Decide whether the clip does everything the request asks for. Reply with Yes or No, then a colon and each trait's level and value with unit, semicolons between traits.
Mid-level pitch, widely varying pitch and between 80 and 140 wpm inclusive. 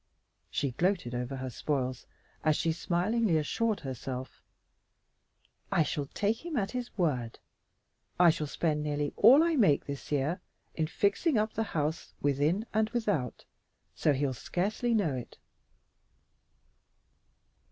Yes: medium, 160 Hz; wide, 7.2 semitones; slow, 135 wpm